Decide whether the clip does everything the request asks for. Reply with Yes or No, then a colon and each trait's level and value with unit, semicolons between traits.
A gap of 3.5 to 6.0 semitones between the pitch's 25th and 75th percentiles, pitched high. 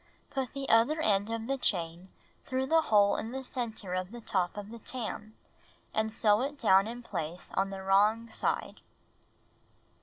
Yes: average, 3.9 semitones; high, 220 Hz